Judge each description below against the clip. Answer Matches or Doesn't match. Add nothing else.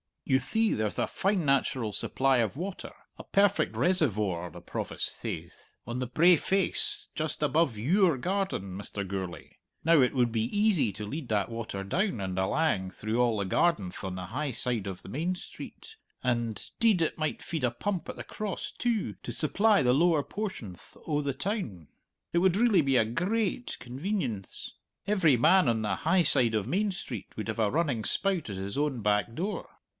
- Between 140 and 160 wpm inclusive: Doesn't match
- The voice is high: Doesn't match